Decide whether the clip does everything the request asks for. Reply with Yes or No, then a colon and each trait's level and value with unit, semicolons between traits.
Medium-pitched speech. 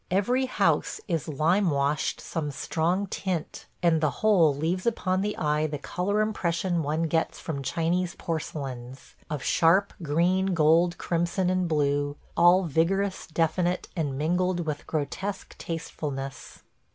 Yes: medium, 165 Hz